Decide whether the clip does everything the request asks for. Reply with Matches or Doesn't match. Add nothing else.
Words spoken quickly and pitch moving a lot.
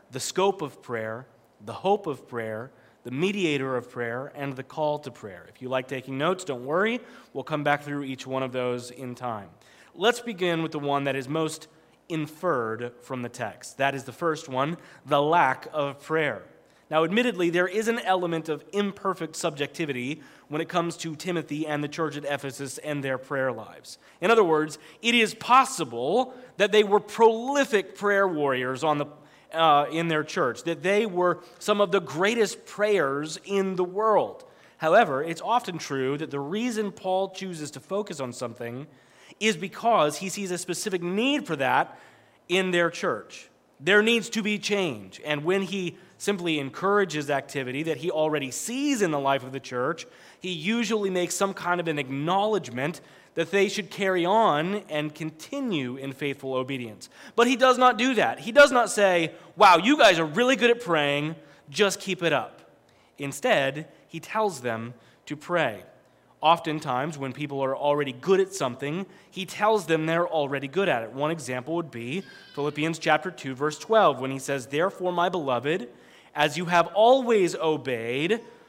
Doesn't match